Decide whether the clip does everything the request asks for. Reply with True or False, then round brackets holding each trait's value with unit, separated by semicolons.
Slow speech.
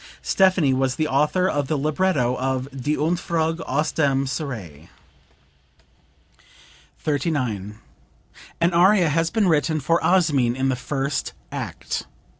True (120 wpm)